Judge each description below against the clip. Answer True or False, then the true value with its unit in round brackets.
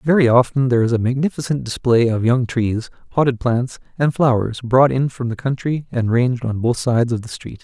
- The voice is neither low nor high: False (125 Hz)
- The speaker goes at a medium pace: False (210 wpm)